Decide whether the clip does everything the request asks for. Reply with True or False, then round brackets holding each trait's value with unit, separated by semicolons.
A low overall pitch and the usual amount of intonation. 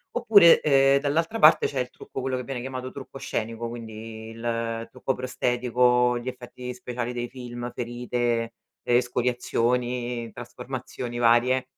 False (125 Hz; 1.3 semitones)